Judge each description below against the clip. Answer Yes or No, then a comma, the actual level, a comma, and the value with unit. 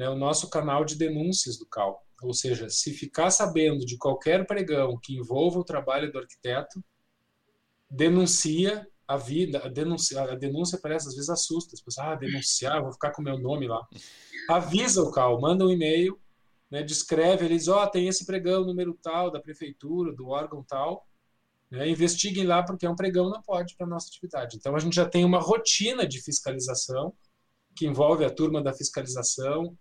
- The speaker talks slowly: No, average, 180 wpm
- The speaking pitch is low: No, medium, 155 Hz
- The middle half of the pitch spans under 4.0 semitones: No, average, 4.6 semitones